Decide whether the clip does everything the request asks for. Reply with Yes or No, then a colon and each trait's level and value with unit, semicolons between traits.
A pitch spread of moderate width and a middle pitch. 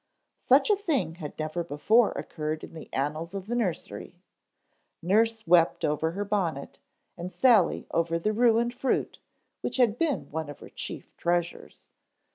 No: wide, 6.0 semitones; medium, 180 Hz